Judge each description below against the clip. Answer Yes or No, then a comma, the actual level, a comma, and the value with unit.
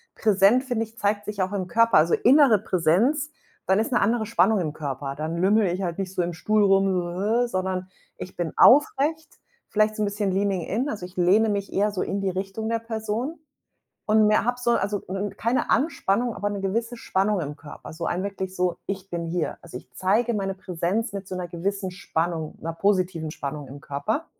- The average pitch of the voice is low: No, high, 195 Hz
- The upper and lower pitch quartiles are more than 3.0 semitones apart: Yes, average, 3.6 semitones